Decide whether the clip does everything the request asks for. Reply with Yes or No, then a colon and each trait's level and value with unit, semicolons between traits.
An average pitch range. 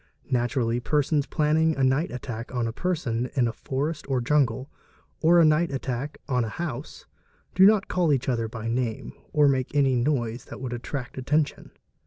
Yes: average, 3.9 semitones